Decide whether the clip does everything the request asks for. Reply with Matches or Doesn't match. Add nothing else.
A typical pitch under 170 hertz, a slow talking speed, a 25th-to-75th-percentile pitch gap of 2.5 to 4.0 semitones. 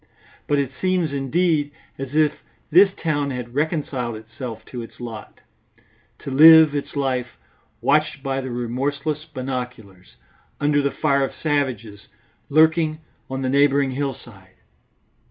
Matches